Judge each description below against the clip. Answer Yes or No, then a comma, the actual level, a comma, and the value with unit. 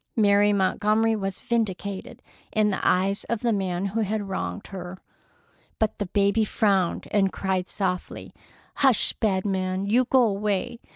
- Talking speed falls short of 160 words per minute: Yes, average, 150 wpm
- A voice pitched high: Yes, high, 200 Hz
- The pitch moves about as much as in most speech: No, narrow, 2.2 semitones